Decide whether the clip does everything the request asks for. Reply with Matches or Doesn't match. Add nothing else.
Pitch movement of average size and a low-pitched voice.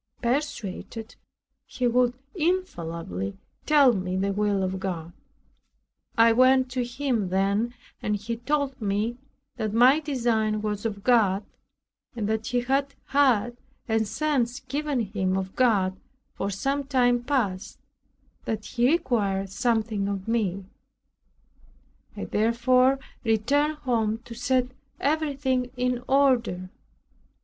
Doesn't match